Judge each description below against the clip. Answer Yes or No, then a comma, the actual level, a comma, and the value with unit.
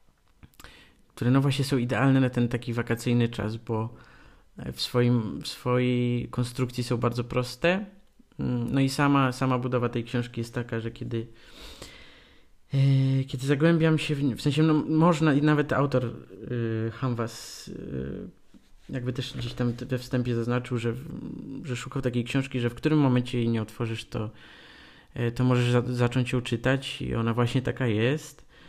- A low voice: Yes, low, 125 Hz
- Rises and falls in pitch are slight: Yes, narrow, 2.3 semitones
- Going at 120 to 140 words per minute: No, fast, 160 wpm